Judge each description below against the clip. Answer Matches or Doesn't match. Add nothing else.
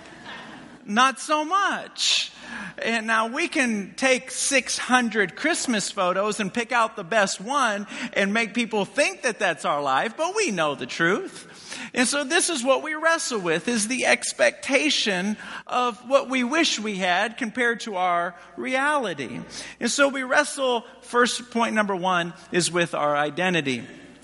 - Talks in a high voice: Matches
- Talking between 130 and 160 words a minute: Matches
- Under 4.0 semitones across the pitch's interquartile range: Doesn't match